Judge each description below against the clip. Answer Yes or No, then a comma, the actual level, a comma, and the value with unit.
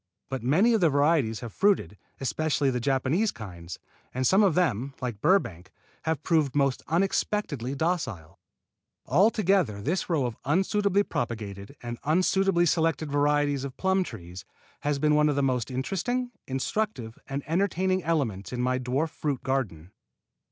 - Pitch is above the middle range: No, medium, 145 Hz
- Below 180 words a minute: Yes, average, 150 wpm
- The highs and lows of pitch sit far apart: Yes, wide, 6.1 semitones